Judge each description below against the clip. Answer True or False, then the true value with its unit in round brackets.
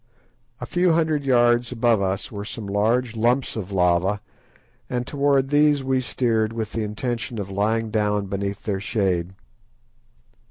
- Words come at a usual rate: True (150 wpm)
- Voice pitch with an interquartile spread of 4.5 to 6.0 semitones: False (3.8 semitones)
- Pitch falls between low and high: False (115 Hz)